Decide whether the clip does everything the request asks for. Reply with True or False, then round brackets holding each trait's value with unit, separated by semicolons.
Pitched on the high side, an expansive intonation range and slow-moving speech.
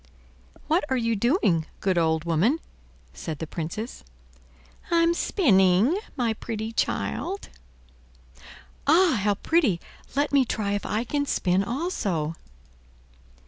True (220 Hz; 7.8 semitones; 115 wpm)